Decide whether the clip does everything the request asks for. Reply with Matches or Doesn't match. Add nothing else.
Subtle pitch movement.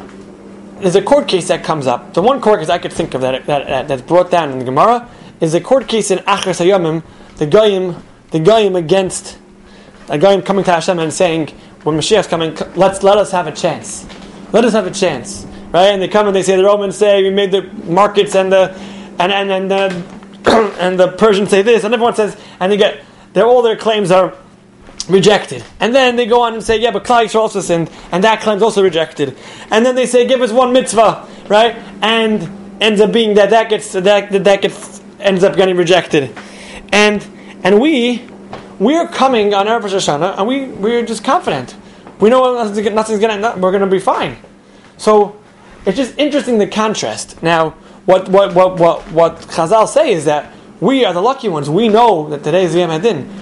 Doesn't match